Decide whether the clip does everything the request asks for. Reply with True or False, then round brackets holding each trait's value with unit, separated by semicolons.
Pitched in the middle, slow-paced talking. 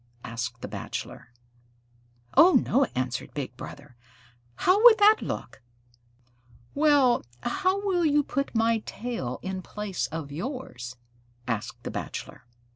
False (225 Hz; 120 wpm)